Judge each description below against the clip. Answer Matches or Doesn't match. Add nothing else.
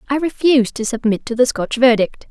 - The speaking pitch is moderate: Doesn't match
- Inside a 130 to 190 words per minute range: Doesn't match